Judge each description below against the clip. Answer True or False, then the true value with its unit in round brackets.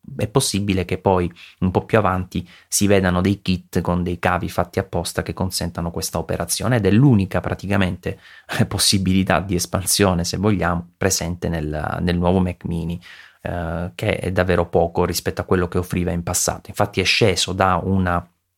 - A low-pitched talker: True (90 Hz)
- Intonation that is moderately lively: False (1.8 semitones)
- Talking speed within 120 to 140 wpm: False (170 wpm)